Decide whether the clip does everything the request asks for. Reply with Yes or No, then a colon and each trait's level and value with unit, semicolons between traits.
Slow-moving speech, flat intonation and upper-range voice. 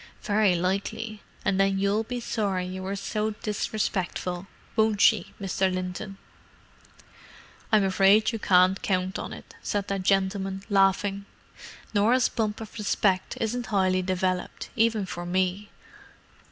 Yes: slow, 130 wpm; narrow, 2.2 semitones; high, 195 Hz